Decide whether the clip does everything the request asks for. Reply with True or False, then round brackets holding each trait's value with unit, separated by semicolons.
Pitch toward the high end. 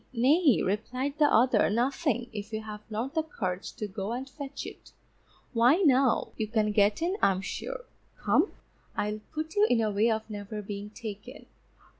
True (225 Hz)